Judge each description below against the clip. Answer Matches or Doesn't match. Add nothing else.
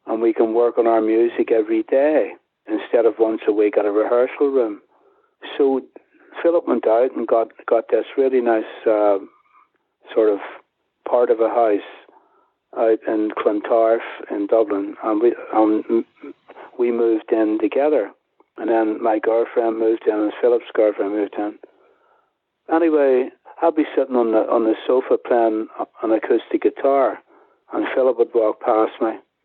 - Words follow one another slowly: Doesn't match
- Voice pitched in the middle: Matches